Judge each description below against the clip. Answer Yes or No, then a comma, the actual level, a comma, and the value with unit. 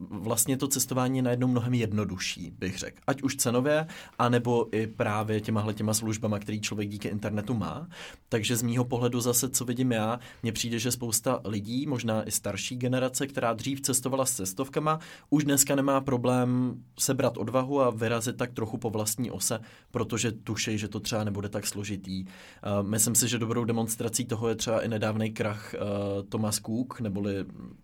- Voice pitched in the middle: No, low, 115 Hz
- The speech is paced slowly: No, fast, 170 wpm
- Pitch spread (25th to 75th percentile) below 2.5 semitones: No, average, 2.8 semitones